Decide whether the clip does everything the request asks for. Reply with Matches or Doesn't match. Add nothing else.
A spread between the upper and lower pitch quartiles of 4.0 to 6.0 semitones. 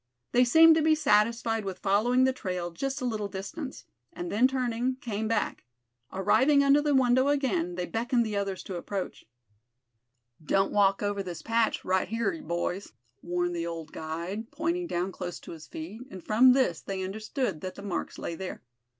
Matches